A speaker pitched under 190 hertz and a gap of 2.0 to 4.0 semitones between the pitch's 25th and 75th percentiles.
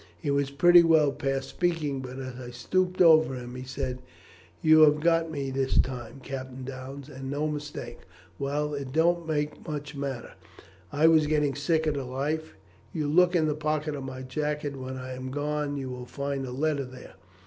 Yes: medium, 140 Hz; average, 2.7 semitones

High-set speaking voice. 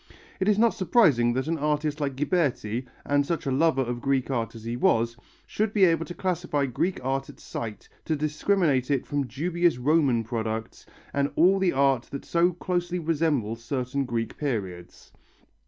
No: medium, 140 Hz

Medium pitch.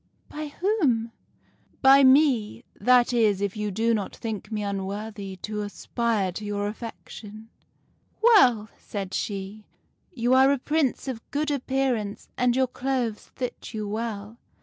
No: high, 225 Hz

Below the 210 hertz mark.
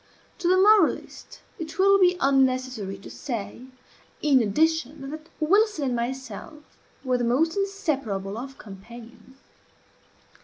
No: very high, 270 Hz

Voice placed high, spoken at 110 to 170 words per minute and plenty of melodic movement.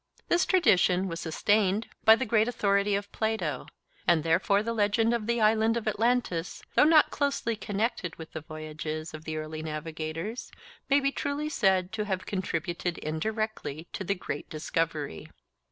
Yes: high, 200 Hz; average, 160 wpm; wide, 5.7 semitones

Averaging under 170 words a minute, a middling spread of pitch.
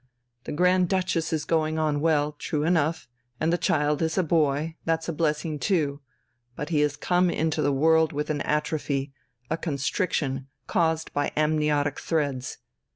No: average, 160 wpm; narrow, 1.9 semitones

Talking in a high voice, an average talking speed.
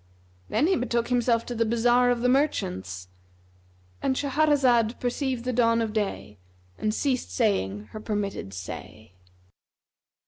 No: high, 230 Hz; slow, 130 wpm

